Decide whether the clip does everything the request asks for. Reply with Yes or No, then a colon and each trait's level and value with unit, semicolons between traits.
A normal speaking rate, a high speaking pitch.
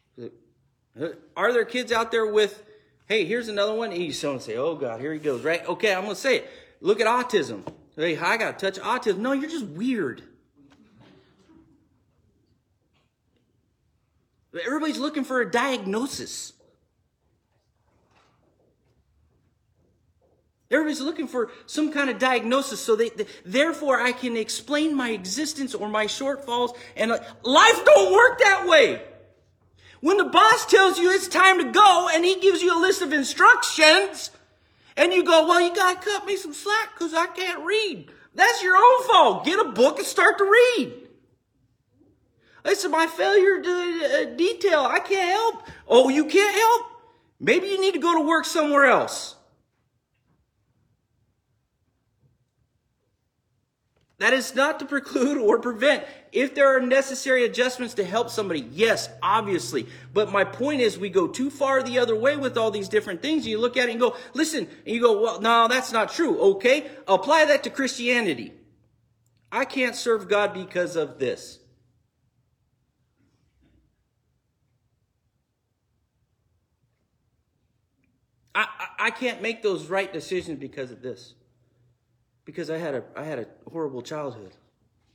Yes: average, 150 wpm; very high, 255 Hz